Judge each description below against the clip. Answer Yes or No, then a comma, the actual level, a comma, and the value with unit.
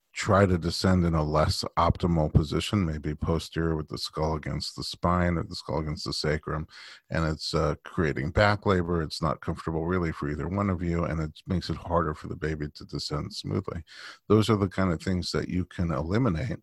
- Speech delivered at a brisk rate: Yes, fast, 210 wpm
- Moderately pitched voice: No, very low, 85 Hz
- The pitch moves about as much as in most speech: Yes, average, 3.2 semitones